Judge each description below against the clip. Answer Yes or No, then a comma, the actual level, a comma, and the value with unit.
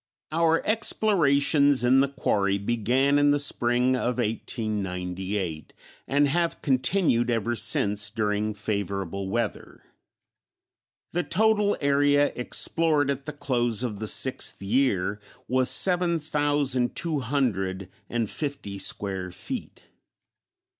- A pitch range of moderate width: No, wide, 5.8 semitones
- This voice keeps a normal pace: No, slow, 115 wpm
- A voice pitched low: Yes, low, 125 Hz